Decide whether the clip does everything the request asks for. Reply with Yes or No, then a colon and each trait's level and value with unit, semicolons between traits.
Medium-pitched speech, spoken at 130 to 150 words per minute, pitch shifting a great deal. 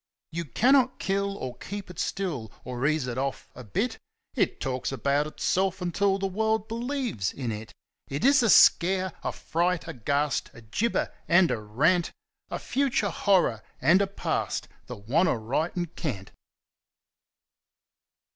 Yes: medium, 170 Hz; average, 145 wpm; wide, 7.2 semitones